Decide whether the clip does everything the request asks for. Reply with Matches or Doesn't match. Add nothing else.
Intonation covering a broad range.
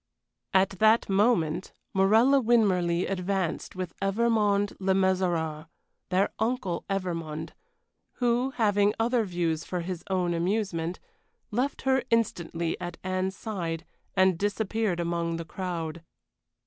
Doesn't match